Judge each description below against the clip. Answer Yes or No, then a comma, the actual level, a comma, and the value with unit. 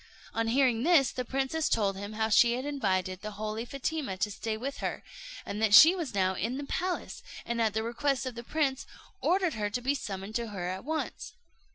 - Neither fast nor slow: No, fast, 215 wpm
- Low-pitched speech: No, high, 235 Hz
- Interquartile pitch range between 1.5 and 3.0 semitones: No, average, 4.8 semitones